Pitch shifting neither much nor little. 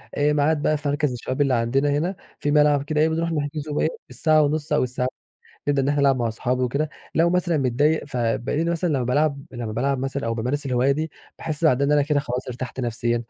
Yes: average, 3.1 semitones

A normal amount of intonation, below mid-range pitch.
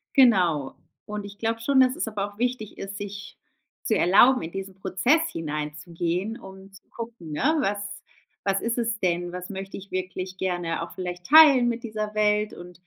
No: average, 4.2 semitones; high, 195 Hz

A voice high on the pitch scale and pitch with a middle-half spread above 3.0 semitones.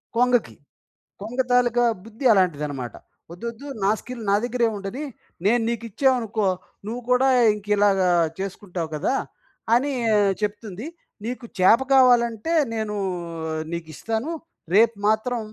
Yes: high, 225 Hz; average, 3.5 semitones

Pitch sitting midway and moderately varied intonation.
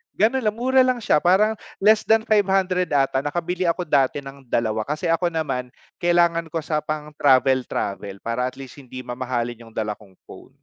No: medium, 150 Hz; wide, 6.2 semitones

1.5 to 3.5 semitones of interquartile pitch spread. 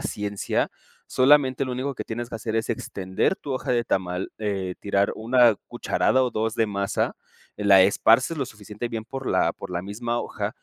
No: average, 3.9 semitones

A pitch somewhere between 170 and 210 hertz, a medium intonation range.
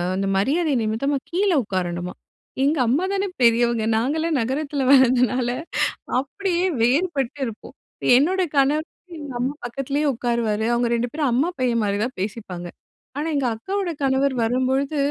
No: very high, 260 Hz; average, 4.1 semitones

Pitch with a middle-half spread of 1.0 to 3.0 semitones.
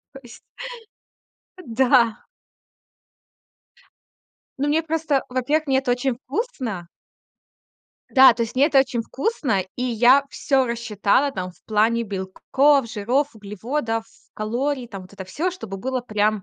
No: average, 4.1 semitones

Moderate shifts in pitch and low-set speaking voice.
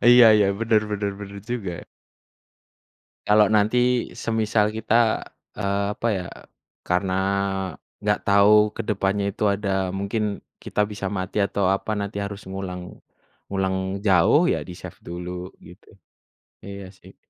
No: narrow, 1.8 semitones; low, 100 Hz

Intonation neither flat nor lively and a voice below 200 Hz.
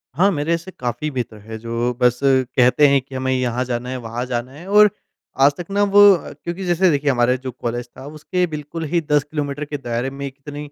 Yes: average, 3.7 semitones; low, 135 Hz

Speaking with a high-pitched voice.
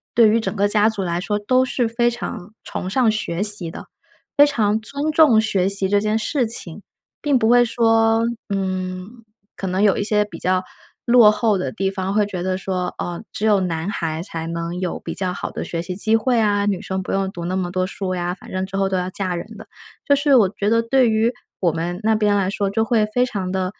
Yes: high, 205 Hz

